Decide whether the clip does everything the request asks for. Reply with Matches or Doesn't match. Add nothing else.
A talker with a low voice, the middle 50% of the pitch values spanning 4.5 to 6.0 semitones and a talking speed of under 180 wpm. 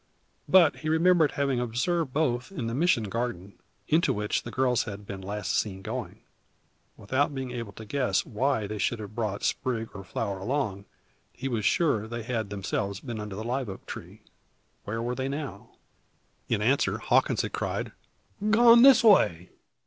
Matches